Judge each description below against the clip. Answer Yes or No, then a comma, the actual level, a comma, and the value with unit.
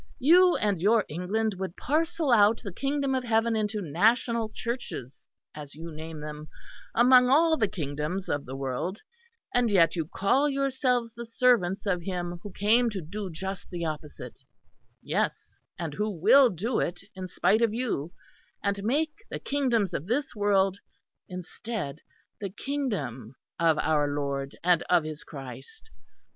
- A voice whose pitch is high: Yes, high, 200 Hz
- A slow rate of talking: No, average, 155 wpm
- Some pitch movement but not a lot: No, wide, 6.5 semitones